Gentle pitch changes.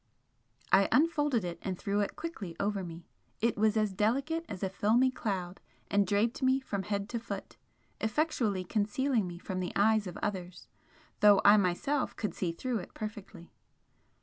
No: average, 3.8 semitones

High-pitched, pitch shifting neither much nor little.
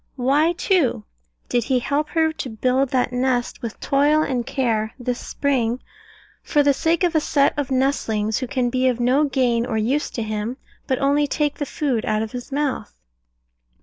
Yes: very high, 260 Hz; average, 3.2 semitones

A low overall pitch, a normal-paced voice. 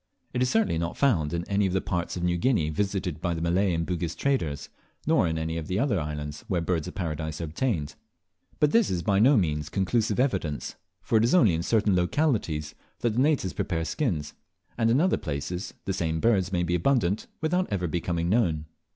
No: very low, 90 Hz; fast, 210 wpm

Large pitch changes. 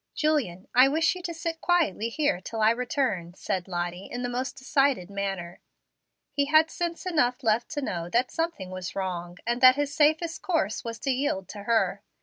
Yes: wide, 7.6 semitones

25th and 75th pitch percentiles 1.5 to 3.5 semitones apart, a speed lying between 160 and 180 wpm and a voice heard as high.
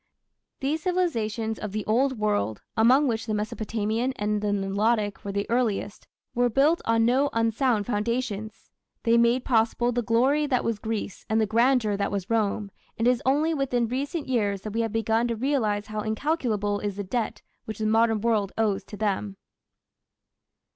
Yes: average, 2.8 semitones; average, 175 wpm; high, 225 Hz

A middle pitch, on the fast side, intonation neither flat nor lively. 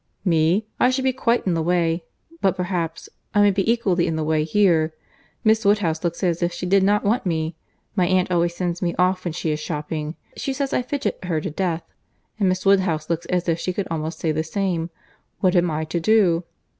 Yes: medium, 175 Hz; fast, 220 wpm; average, 3.2 semitones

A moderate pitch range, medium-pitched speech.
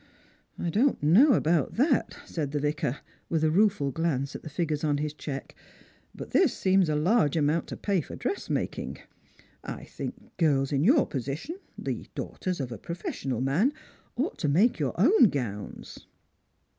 No: wide, 5.8 semitones; medium, 155 Hz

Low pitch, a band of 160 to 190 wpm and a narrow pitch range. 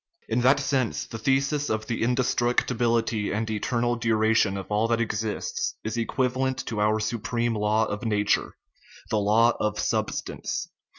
Yes: low, 115 Hz; average, 170 wpm; narrow, 2.1 semitones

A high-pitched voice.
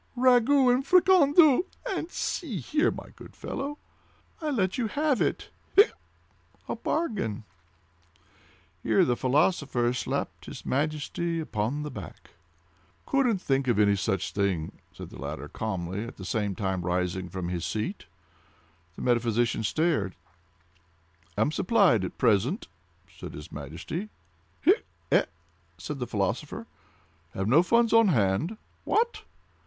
No: medium, 140 Hz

